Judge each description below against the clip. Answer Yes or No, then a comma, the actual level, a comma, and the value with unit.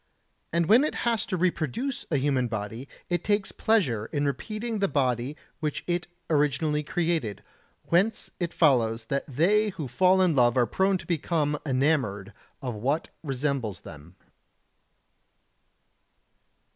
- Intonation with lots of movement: Yes, wide, 6.2 semitones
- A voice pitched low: No, medium, 150 Hz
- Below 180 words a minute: Yes, slow, 135 wpm